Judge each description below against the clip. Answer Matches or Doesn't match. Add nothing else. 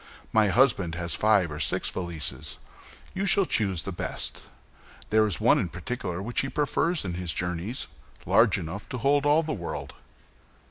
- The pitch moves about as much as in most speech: Doesn't match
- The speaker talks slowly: Doesn't match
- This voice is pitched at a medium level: Doesn't match